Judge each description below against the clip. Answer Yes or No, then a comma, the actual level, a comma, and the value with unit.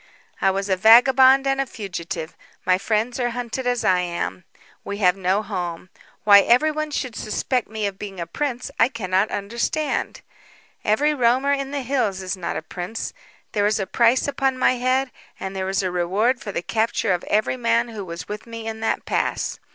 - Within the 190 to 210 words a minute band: Yes, average, 195 wpm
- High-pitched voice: Yes, high, 220 Hz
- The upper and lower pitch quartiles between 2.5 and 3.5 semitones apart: No, average, 4.8 semitones